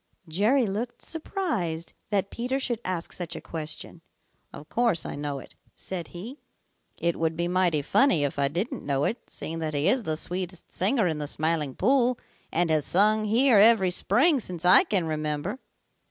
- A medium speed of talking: Yes, average, 180 wpm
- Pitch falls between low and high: Yes, medium, 180 Hz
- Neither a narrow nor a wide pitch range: No, wide, 6.4 semitones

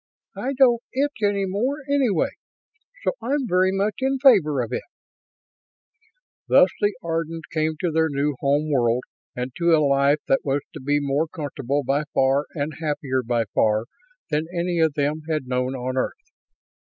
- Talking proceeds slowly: No, average, 170 wpm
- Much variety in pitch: Yes, wide, 5.9 semitones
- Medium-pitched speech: Yes, medium, 155 Hz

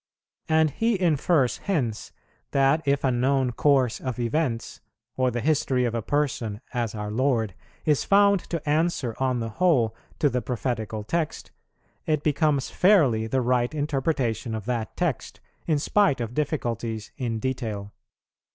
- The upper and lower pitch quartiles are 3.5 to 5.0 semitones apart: Yes, average, 4.7 semitones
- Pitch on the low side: Yes, low, 130 Hz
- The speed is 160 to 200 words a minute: No, average, 150 wpm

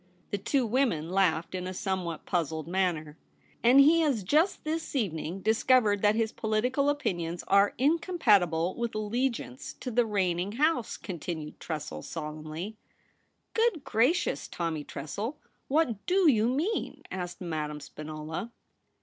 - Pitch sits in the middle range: No, high, 205 Hz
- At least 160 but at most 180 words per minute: No, average, 145 wpm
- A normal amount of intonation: No, wide, 7.4 semitones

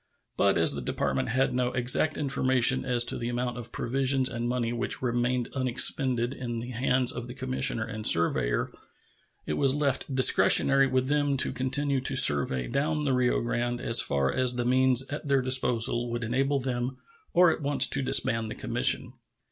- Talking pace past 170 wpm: Yes, average, 180 wpm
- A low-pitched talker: Yes, low, 125 Hz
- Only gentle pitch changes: Yes, narrow, 2.0 semitones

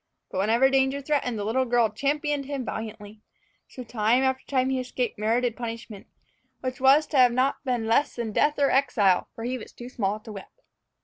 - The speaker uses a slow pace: No, average, 195 wpm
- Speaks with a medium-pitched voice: No, high, 245 Hz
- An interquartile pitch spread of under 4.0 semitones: Yes, average, 3.2 semitones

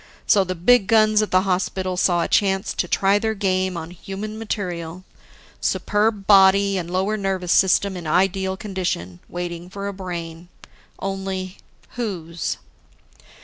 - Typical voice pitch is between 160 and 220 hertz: Yes, high, 190 Hz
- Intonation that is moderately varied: No, narrow, 2.1 semitones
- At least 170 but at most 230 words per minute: No, average, 145 wpm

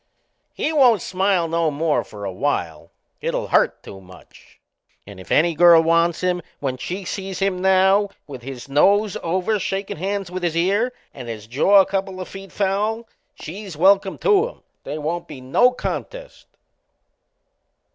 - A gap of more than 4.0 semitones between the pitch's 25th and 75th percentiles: Yes, average, 5.0 semitones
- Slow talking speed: No, average, 165 wpm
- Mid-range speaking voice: Yes, medium, 180 Hz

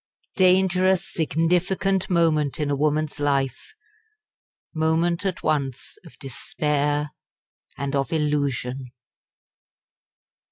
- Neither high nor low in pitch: Yes, medium, 155 Hz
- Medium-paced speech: No, slow, 85 wpm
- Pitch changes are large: No, average, 3.5 semitones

